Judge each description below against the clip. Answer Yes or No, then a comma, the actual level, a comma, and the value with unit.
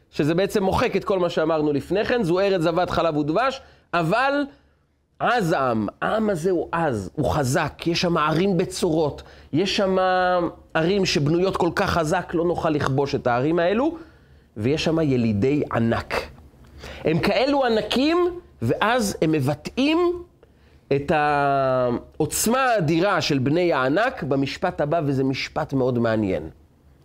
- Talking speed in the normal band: Yes, average, 135 wpm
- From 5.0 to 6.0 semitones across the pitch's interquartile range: Yes, average, 5.3 semitones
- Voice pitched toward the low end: No, medium, 165 Hz